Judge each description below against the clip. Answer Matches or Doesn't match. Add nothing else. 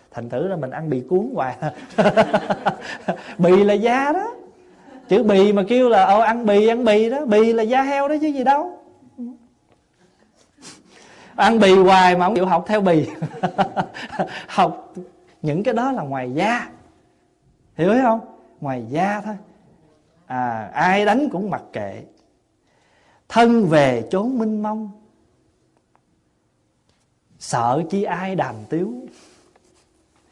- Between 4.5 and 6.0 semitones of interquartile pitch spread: Matches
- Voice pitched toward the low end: Doesn't match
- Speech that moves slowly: Matches